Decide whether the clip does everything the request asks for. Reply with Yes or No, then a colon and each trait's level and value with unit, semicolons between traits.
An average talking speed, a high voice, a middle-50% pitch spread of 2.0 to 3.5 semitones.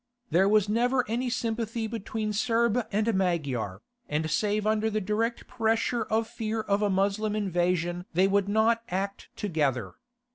Yes: average, 150 wpm; high, 210 Hz; average, 3.2 semitones